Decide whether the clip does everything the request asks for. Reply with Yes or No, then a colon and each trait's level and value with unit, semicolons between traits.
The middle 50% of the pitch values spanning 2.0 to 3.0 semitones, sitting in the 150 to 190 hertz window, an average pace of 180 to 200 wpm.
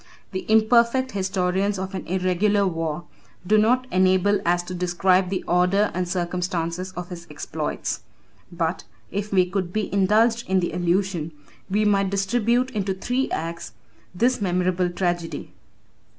No: narrow, 2.5 semitones; medium, 185 Hz; average, 145 wpm